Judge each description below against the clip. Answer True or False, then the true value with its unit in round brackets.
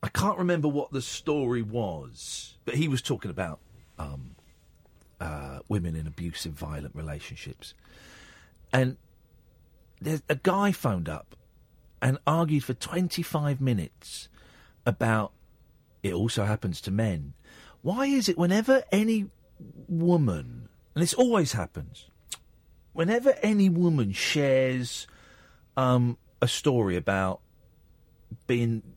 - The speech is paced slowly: True (115 wpm)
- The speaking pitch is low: True (120 Hz)